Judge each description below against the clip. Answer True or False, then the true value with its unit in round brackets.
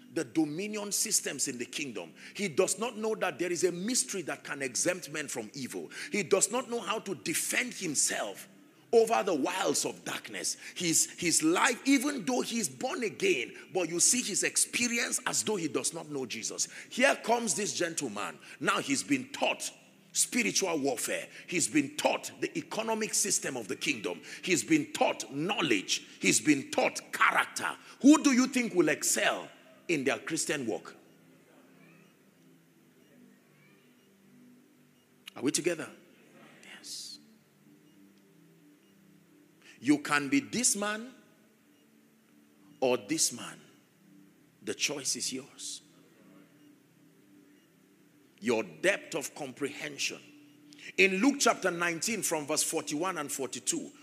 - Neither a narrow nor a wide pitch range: False (8.9 semitones)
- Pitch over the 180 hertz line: True (190 Hz)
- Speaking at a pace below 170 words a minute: True (135 wpm)